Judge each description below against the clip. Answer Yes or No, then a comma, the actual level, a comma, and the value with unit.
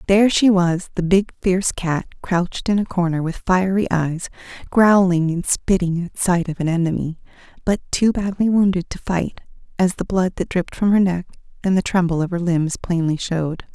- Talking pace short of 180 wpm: No, average, 190 wpm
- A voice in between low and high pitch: Yes, medium, 180 Hz